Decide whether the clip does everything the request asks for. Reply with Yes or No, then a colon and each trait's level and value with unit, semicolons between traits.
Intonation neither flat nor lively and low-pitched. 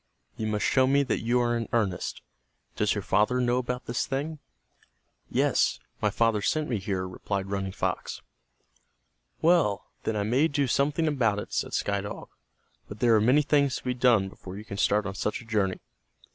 Yes: average, 4.2 semitones; low, 115 Hz